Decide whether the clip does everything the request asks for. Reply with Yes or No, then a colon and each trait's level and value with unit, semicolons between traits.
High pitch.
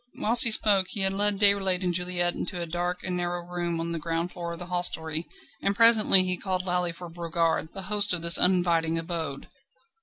No: medium, 175 Hz